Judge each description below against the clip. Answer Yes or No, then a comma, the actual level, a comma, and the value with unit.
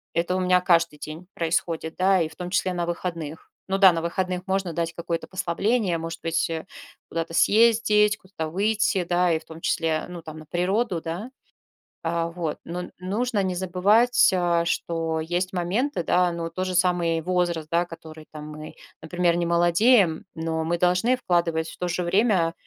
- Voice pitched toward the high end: No, medium, 175 Hz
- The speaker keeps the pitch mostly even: Yes, narrow, 2.1 semitones